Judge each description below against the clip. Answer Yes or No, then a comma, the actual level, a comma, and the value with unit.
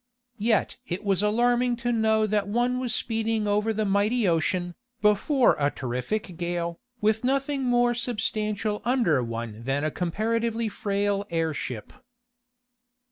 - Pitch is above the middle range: Yes, high, 210 Hz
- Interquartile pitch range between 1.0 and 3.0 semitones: No, average, 4.9 semitones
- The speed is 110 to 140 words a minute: Yes, slow, 135 wpm